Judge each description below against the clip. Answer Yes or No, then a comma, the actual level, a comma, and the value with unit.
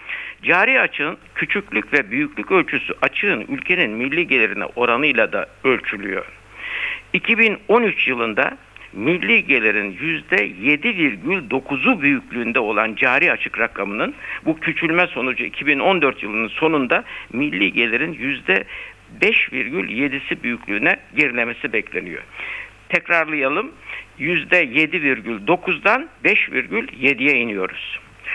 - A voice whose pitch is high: No, medium, 170 Hz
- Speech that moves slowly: Yes, slow, 85 wpm